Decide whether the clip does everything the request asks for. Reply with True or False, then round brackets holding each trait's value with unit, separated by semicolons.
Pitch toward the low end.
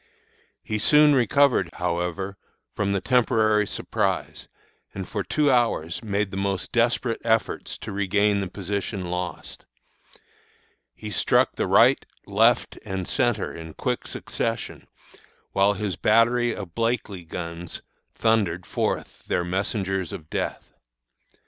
True (100 Hz)